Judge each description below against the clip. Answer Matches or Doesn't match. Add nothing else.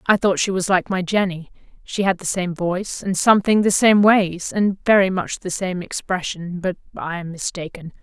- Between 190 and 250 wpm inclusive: Matches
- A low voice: Doesn't match